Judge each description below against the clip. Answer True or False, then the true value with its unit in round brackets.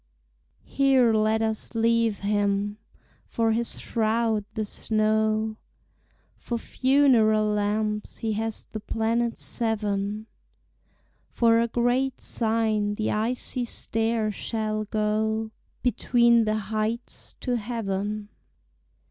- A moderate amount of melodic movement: False (1.5 semitones)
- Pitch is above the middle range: True (220 Hz)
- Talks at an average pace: False (100 wpm)